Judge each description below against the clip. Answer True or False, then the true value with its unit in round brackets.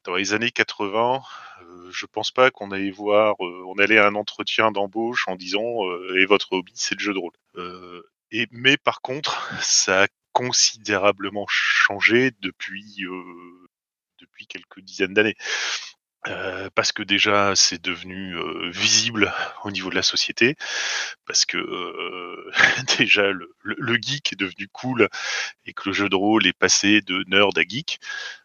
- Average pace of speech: True (170 wpm)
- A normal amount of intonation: True (3.7 semitones)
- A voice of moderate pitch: False (105 Hz)